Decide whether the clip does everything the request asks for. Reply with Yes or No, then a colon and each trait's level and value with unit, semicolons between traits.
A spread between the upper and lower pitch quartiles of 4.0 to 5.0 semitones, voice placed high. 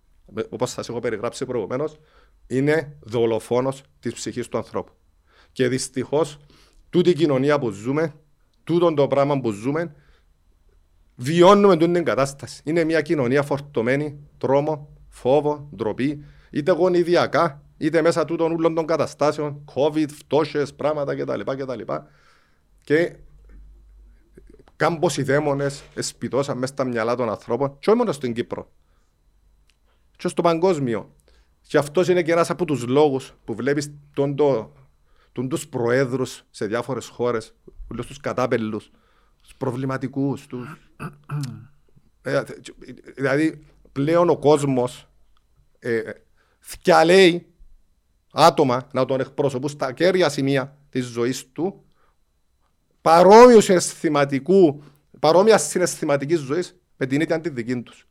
No: average, 4.3 semitones; medium, 140 Hz